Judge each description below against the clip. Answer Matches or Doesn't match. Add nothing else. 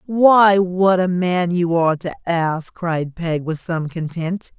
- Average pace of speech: Matches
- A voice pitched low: Doesn't match